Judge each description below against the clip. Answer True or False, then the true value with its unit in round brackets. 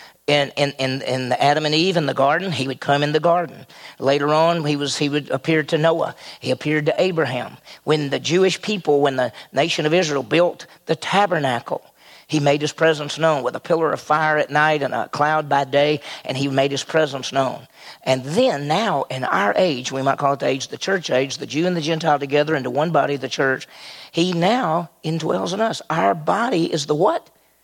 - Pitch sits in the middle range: True (150 Hz)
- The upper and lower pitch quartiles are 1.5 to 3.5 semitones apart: True (3.1 semitones)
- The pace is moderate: False (220 wpm)